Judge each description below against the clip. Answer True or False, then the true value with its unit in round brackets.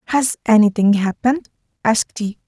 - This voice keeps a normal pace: False (120 wpm)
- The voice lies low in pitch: False (225 Hz)